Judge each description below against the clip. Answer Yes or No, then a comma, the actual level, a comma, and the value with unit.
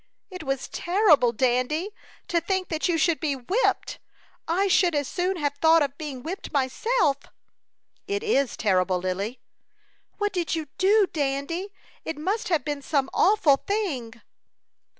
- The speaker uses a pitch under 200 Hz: No, very high, 315 Hz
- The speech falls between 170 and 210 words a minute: No, average, 150 wpm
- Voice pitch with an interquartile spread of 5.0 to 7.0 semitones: Yes, wide, 5.5 semitones